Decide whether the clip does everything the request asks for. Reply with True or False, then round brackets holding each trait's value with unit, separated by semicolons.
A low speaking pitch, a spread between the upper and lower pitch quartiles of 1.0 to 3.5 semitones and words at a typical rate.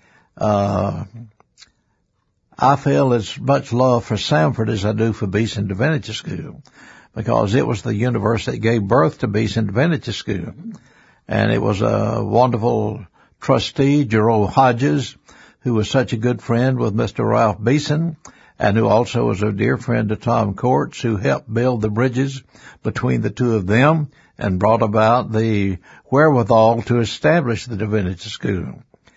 True (115 Hz; 3.1 semitones; 155 wpm)